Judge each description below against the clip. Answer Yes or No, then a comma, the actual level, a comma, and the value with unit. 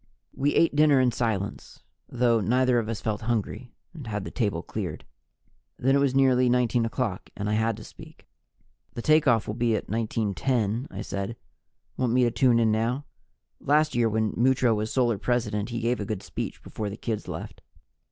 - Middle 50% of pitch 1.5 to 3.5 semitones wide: Yes, average, 2.8 semitones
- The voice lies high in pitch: No, low, 115 Hz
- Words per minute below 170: No, average, 190 wpm